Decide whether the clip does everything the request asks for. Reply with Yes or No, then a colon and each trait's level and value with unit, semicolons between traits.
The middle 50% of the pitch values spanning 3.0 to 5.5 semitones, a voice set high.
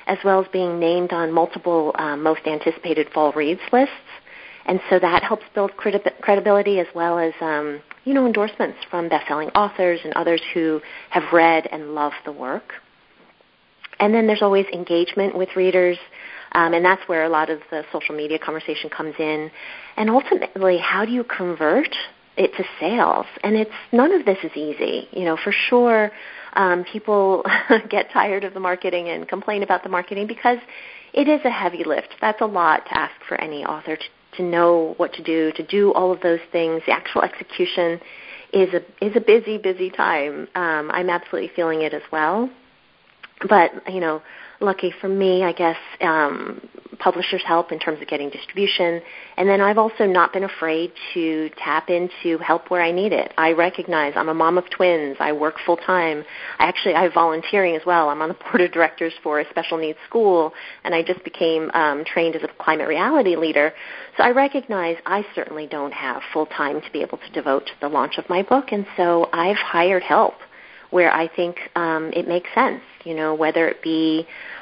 No: average, 3.3 semitones; medium, 175 Hz